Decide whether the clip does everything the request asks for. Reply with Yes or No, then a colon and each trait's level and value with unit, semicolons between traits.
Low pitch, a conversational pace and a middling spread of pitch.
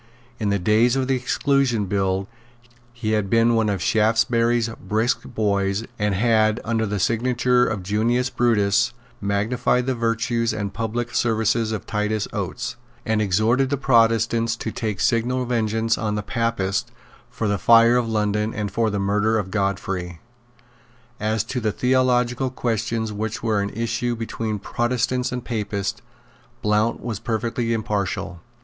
No: low, 110 Hz; average, 150 wpm; narrow, 2.2 semitones